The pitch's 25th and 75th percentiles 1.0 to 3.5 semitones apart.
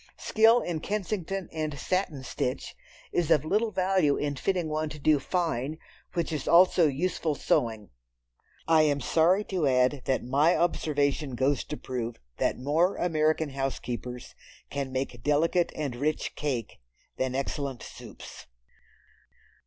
No: average, 4.2 semitones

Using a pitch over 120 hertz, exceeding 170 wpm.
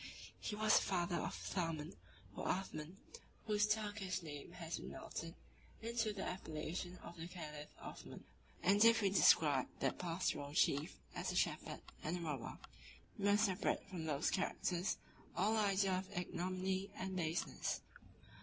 No: medium, 185 Hz; average, 150 wpm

